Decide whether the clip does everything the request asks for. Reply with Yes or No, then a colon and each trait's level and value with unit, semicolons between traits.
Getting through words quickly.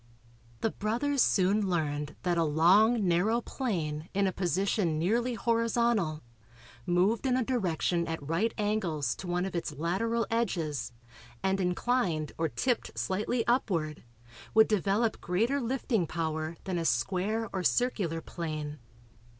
No: slow, 135 wpm